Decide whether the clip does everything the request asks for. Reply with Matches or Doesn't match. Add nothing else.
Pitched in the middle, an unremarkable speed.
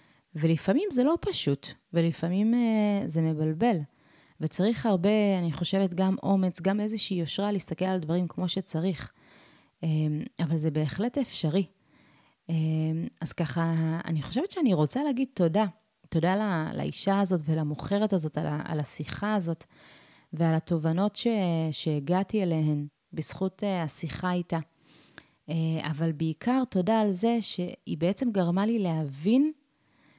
Matches